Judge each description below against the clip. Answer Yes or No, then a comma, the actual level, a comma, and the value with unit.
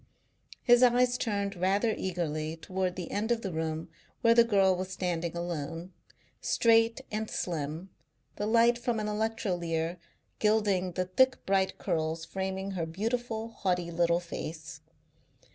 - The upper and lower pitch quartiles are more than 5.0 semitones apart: No, average, 4.5 semitones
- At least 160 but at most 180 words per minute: No, average, 140 wpm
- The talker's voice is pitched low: No, high, 190 Hz